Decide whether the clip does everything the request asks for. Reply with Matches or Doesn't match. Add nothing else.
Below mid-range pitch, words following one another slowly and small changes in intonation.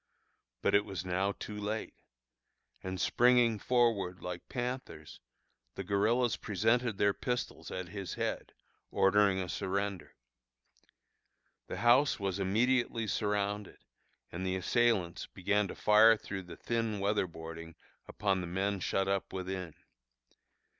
Doesn't match